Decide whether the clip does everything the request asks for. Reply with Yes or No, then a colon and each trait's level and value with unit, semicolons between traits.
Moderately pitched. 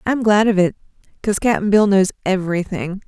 No: high, 200 Hz